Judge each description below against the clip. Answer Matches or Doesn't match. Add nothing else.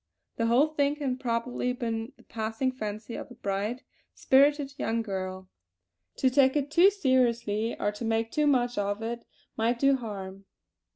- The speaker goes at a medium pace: Matches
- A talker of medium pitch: Doesn't match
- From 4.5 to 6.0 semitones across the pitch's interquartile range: Doesn't match